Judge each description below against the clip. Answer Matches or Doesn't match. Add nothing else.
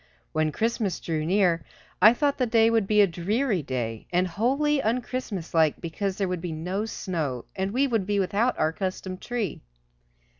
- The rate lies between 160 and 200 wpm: Matches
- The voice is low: Doesn't match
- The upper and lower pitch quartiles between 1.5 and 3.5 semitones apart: Doesn't match